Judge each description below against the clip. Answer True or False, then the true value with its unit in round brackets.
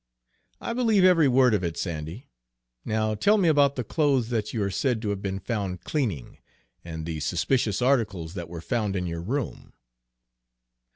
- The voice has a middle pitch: False (110 Hz)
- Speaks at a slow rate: False (175 wpm)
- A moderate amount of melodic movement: False (6.8 semitones)